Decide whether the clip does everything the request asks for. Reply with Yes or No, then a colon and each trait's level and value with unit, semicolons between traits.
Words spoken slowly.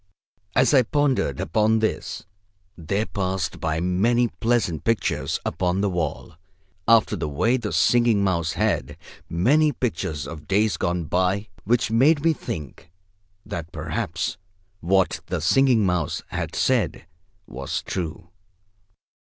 Yes: slow, 125 wpm